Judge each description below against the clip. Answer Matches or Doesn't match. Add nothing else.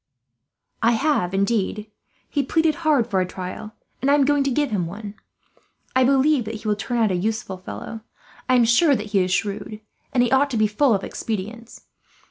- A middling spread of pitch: Matches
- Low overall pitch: Doesn't match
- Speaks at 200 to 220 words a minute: Matches